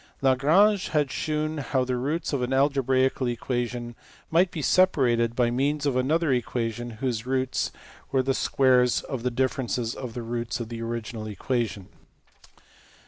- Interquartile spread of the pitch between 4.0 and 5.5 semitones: No, average, 2.7 semitones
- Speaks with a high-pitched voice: No, low, 130 Hz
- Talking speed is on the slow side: No, average, 155 wpm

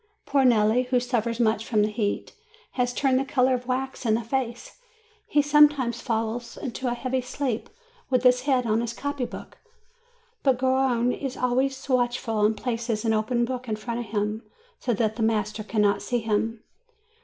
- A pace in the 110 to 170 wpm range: No, average, 185 wpm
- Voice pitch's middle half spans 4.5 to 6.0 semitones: No, average, 2.7 semitones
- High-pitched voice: Yes, high, 240 Hz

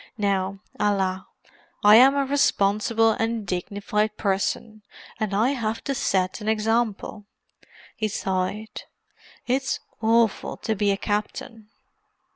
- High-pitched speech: Yes, high, 215 Hz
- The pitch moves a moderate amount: No, narrow, 2.2 semitones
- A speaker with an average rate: No, slow, 115 wpm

